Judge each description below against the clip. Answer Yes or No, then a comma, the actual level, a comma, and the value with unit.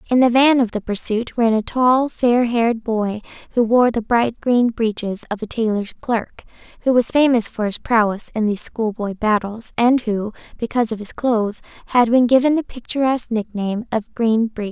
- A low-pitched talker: No, high, 230 Hz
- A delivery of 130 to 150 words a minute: No, average, 190 wpm